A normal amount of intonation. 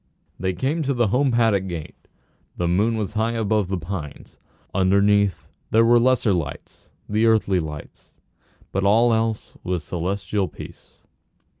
Yes: average, 3.6 semitones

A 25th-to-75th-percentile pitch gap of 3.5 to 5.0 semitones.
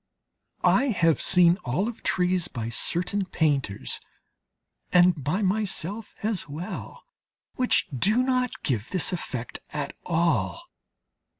No: wide, 5.4 semitones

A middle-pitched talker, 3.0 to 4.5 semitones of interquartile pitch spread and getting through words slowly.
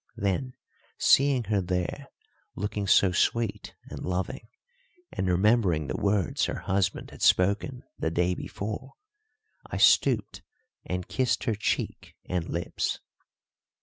No: low, 100 Hz; average, 3.5 semitones; slow, 120 wpm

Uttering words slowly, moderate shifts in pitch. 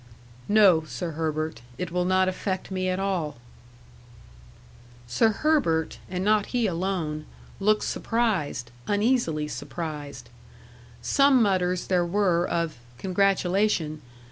Yes: slow, 110 wpm; average, 4.3 semitones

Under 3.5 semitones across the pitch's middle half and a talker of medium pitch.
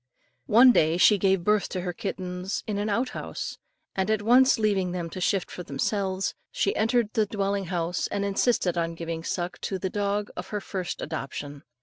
No: average, 2.9 semitones; high, 195 Hz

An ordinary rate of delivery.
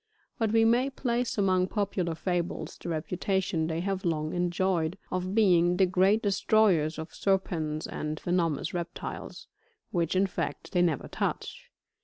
Yes: average, 145 wpm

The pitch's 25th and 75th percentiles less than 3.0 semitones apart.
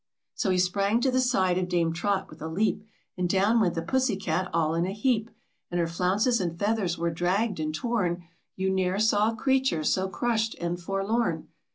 No: average, 4.1 semitones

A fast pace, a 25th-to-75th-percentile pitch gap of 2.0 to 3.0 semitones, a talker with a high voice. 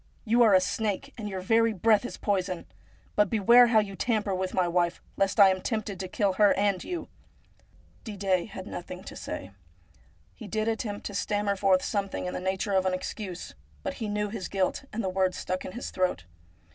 Yes: fast, 210 wpm; narrow, 2.5 semitones; high, 200 Hz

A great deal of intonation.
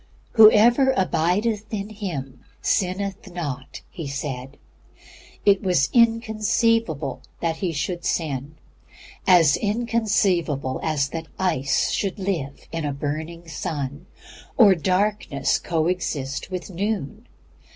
Yes: wide, 6.1 semitones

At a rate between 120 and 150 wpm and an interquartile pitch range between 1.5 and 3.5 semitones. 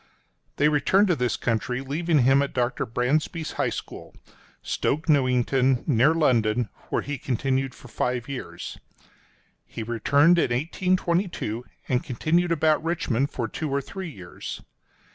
No: average, 140 wpm; average, 4.2 semitones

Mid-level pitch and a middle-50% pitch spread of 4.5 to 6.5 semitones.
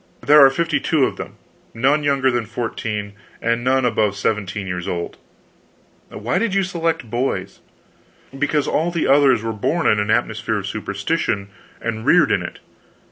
No: low, 120 Hz; wide, 5.5 semitones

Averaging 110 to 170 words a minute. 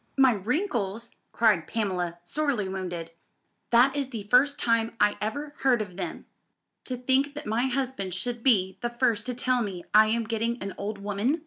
No: average, 180 wpm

